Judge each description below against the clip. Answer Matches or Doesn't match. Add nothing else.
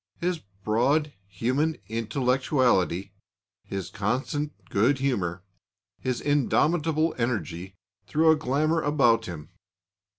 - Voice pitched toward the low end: Matches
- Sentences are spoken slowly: Matches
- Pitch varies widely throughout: Matches